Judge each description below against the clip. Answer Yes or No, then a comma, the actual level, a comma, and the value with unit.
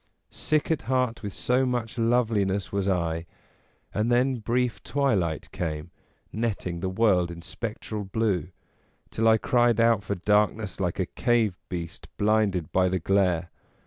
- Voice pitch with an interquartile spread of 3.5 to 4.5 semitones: Yes, average, 4.2 semitones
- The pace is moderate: Yes, average, 150 wpm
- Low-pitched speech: Yes, low, 105 Hz